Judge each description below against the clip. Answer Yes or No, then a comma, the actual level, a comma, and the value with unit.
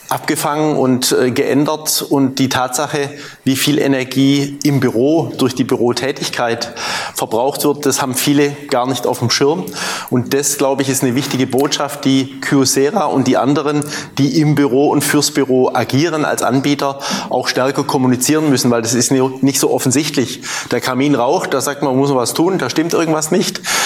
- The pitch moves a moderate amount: No, narrow, 1.9 semitones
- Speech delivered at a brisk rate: No, average, 175 wpm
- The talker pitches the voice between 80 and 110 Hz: No, medium, 140 Hz